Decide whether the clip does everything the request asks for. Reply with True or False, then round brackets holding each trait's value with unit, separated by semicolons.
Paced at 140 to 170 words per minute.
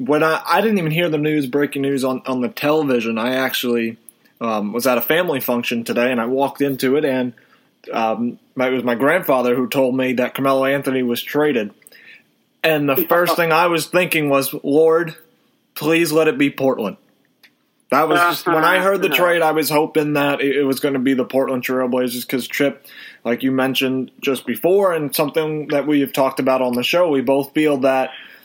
False (205 wpm)